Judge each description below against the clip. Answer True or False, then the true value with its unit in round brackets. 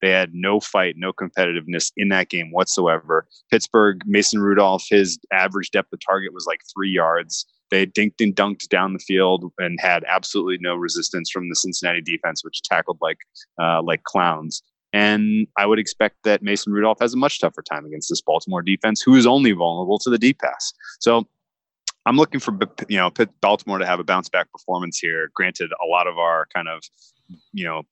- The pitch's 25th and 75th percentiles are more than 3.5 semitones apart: False (3.0 semitones)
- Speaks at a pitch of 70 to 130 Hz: True (95 Hz)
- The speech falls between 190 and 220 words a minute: True (195 wpm)